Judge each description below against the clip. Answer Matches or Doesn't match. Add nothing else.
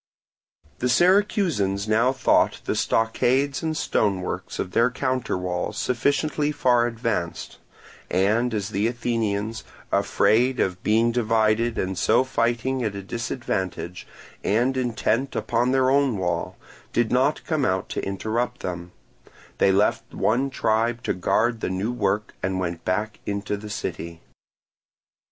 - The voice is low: Matches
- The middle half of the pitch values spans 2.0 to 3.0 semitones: Doesn't match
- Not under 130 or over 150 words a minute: Matches